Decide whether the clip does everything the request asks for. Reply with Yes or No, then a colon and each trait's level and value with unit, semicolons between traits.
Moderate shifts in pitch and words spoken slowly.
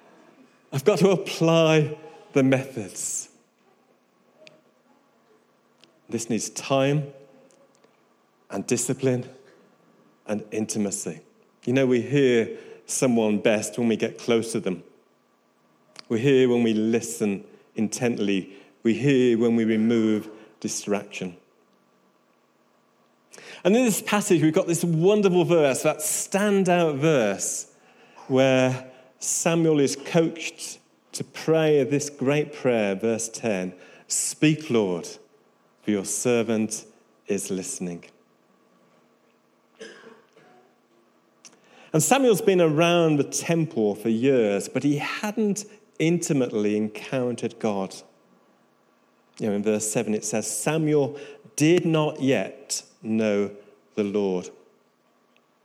No: wide, 6.7 semitones; slow, 100 wpm